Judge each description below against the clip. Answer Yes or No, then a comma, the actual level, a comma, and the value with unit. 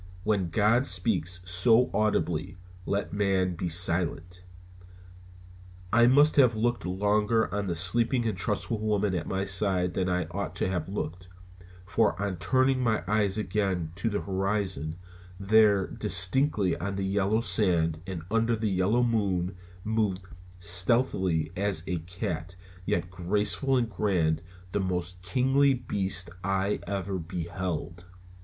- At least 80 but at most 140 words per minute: Yes, slow, 135 wpm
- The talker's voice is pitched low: Yes, very low, 95 Hz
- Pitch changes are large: No, average, 3.1 semitones